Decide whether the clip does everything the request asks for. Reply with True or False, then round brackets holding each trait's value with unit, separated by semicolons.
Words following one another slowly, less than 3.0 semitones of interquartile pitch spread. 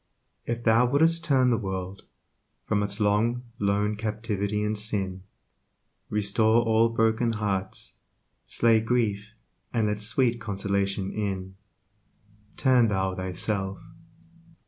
True (110 wpm; 2.6 semitones)